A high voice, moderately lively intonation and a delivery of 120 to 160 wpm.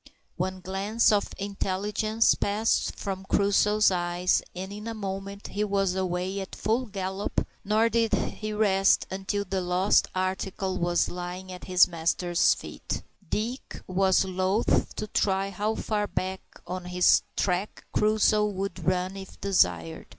No: high, 195 Hz; narrow, 2.1 semitones; average, 145 wpm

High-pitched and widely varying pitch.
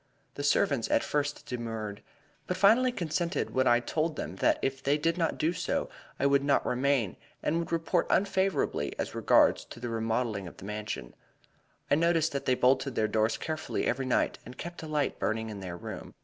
No: low, 135 Hz; wide, 6.3 semitones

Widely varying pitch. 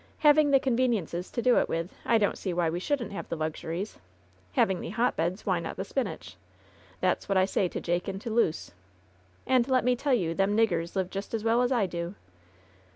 Yes: wide, 5.7 semitones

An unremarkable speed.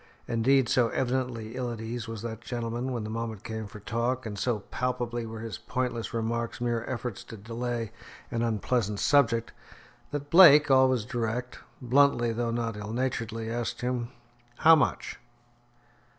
Yes: average, 155 wpm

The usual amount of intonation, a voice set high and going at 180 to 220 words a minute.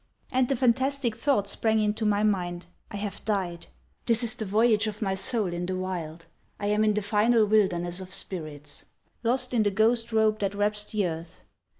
Yes: average, 3.1 semitones; high, 210 Hz; average, 190 wpm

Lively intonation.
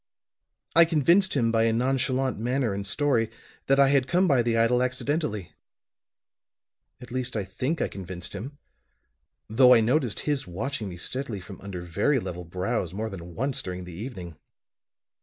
Yes: wide, 5.7 semitones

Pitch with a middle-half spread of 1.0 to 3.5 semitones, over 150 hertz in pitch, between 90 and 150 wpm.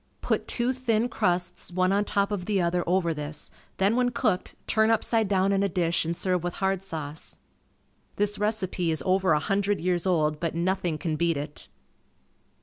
No: average, 3.2 semitones; medium, 185 Hz; average, 185 wpm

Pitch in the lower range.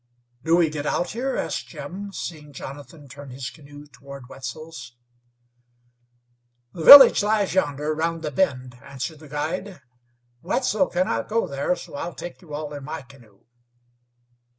No: medium, 150 Hz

